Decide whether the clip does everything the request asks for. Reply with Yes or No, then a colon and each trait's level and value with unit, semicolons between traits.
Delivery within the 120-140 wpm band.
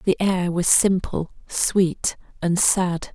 Yes: slow, 135 wpm